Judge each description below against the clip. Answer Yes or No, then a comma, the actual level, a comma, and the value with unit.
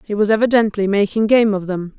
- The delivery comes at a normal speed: No, fast, 210 wpm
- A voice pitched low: No, high, 210 Hz